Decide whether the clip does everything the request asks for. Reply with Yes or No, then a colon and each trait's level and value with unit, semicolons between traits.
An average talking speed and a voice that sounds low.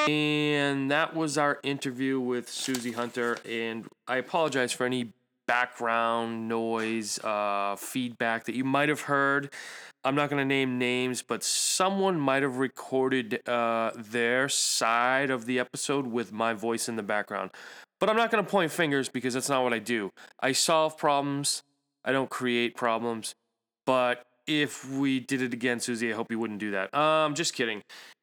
Yes: average, 170 wpm; low, 125 Hz